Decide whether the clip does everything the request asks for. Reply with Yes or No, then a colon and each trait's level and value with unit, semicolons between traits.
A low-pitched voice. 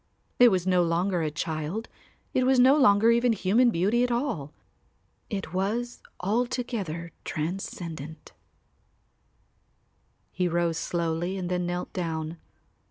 No: medium, 185 Hz